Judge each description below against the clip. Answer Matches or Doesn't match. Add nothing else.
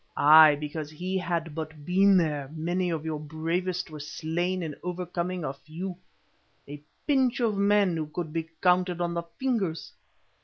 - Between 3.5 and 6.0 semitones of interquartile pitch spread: Doesn't match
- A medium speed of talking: Matches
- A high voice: Doesn't match